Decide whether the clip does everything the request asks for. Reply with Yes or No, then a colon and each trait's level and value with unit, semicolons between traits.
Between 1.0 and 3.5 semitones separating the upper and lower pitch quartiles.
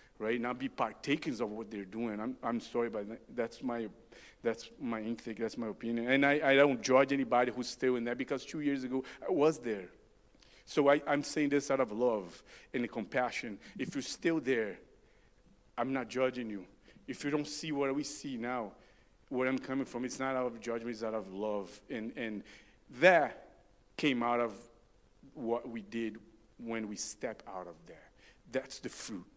Yes: average, 2.9 semitones